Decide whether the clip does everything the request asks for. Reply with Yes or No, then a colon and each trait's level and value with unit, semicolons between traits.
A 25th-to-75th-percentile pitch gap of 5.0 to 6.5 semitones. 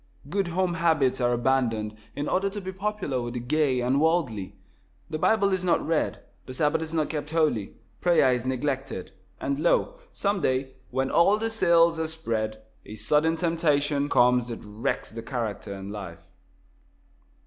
Yes: wide, 5.6 semitones